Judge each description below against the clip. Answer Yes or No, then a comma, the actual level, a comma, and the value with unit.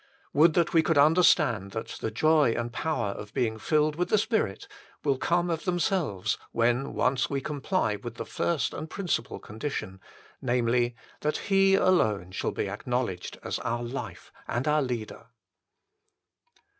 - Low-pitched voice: Yes, low, 130 Hz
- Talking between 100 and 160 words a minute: Yes, average, 155 wpm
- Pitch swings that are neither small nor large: No, wide, 5.9 semitones